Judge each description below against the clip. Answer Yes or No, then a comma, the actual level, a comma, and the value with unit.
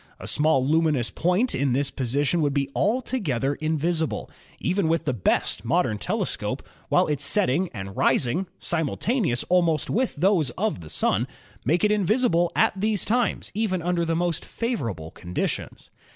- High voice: No, medium, 165 Hz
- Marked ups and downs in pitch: Yes, wide, 5.7 semitones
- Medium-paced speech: Yes, average, 160 wpm